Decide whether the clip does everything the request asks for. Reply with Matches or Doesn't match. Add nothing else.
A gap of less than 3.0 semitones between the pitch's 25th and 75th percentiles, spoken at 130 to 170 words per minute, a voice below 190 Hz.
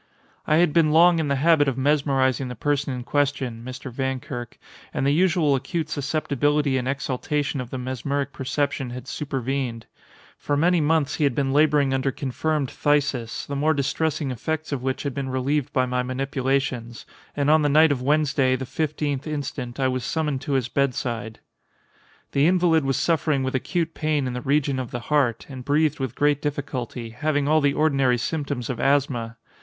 Doesn't match